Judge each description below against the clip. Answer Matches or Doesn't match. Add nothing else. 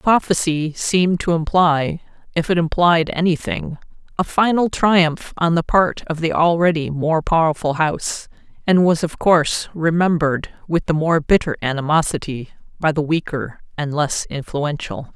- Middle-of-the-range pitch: Matches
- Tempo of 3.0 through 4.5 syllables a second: Doesn't match